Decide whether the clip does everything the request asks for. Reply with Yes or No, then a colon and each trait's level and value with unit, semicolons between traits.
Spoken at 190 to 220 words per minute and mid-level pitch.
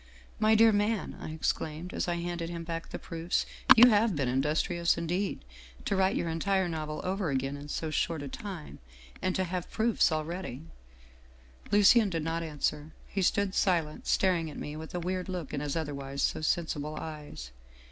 Yes: average, 200 wpm; medium, 165 Hz